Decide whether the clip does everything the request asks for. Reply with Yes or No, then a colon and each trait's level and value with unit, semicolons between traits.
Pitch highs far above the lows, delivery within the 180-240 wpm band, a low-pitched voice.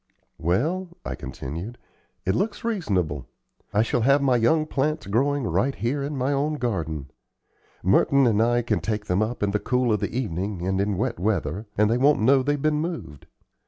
Yes: wide, 6.1 semitones; average, 190 wpm; low, 120 Hz